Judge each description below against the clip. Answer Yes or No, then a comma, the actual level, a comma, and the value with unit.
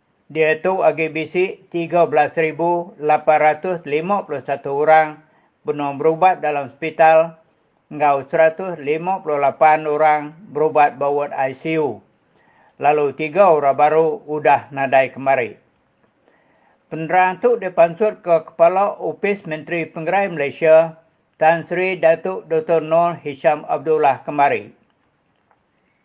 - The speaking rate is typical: No, slow, 90 wpm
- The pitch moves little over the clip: Yes, narrow, 2.3 semitones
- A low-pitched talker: No, medium, 160 Hz